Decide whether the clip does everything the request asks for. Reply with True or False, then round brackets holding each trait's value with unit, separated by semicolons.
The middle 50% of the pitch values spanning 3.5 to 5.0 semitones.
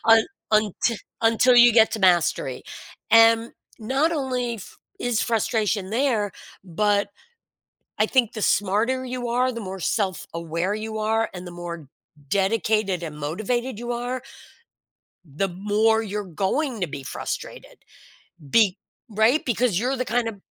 True (3.9 semitones)